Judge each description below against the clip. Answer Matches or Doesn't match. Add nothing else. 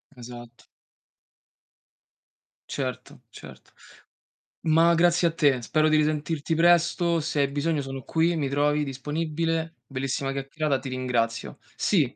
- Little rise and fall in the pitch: Doesn't match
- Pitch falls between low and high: Matches